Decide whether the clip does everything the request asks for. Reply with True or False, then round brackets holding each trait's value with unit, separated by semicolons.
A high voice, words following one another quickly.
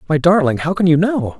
False (165 Hz; 260 wpm)